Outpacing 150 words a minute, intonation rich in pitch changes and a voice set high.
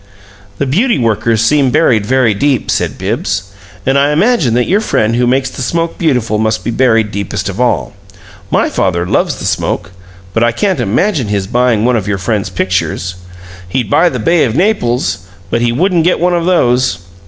No: average, 190 wpm; wide, 5.8 semitones; low, 120 Hz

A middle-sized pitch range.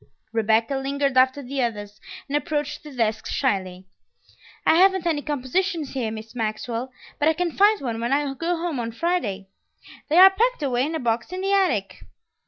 No: wide, 6.5 semitones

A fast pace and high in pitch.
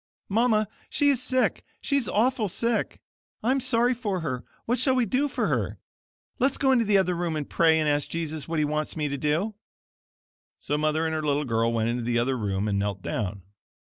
No: fast, 215 wpm; medium, 165 Hz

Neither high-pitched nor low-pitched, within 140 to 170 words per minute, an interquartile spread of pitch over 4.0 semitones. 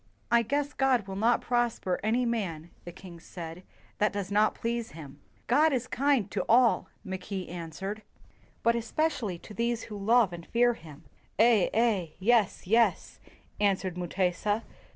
No: high, 210 Hz; average, 165 wpm; average, 4.5 semitones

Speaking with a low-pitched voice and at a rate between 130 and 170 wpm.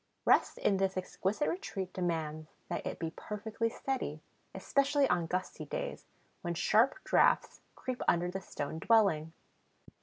No: high, 190 Hz; average, 140 wpm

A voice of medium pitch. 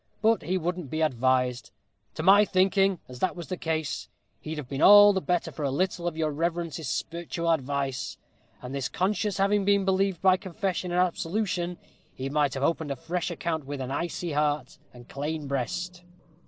Yes: medium, 170 Hz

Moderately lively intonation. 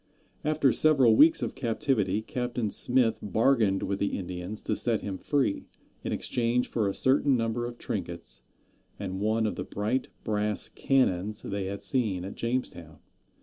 Yes: average, 4.0 semitones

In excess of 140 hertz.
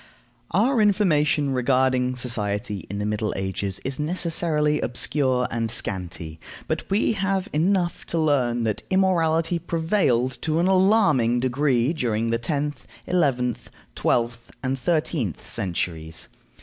No: low, 130 Hz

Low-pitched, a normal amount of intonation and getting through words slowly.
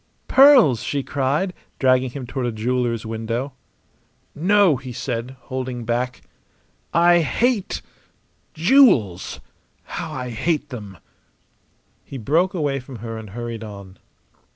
Yes: low, 130 Hz; average, 4.8 semitones; slow, 120 wpm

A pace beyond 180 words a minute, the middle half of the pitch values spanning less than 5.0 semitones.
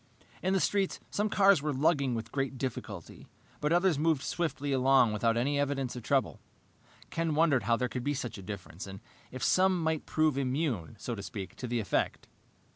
No: average, 195 wpm; average, 5.3 semitones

